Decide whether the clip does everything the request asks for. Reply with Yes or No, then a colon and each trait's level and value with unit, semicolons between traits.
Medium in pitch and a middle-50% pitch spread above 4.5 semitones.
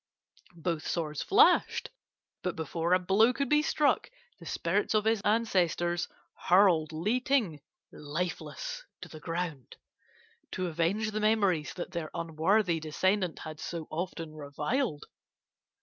Yes: medium, 175 Hz; average, 5.0 semitones